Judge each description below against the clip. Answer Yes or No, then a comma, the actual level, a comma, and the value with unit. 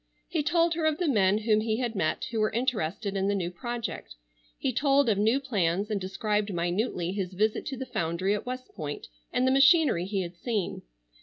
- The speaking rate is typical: No, fast, 210 wpm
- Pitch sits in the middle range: No, high, 215 Hz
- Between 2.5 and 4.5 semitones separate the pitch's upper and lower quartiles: No, average, 5.2 semitones